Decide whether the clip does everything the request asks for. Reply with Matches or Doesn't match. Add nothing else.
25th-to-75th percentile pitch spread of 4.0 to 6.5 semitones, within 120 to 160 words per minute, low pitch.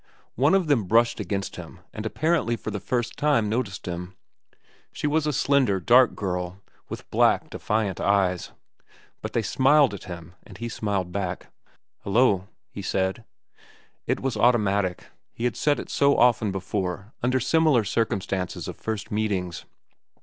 Matches